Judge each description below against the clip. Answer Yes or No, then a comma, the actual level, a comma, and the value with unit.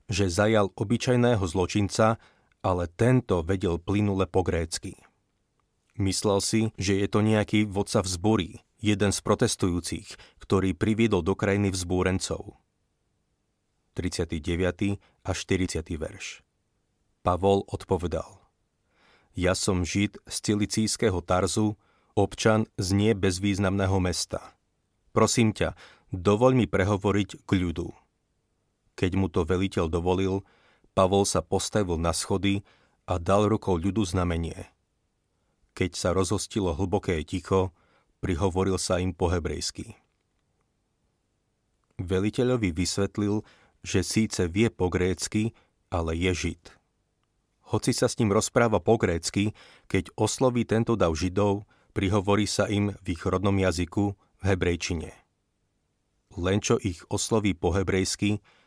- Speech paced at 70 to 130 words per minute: Yes, average, 115 wpm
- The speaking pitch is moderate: No, low, 100 Hz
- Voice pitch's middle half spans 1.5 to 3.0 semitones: Yes, narrow, 2.6 semitones